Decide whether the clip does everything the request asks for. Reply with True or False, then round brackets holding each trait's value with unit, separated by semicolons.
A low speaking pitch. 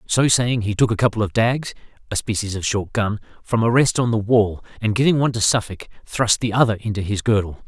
True (110 Hz)